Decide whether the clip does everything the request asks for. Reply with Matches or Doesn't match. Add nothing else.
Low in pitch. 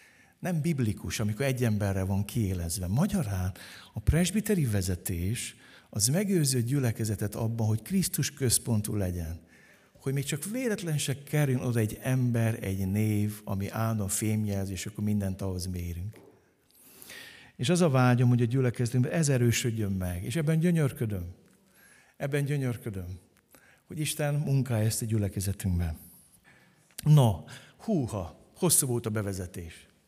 Matches